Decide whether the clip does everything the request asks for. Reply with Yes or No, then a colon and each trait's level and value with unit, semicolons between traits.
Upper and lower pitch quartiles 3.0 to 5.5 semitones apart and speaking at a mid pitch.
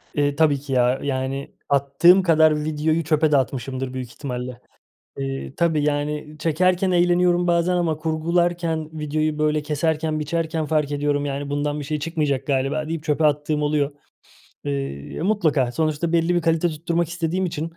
No: narrow, 2.5 semitones; medium, 155 Hz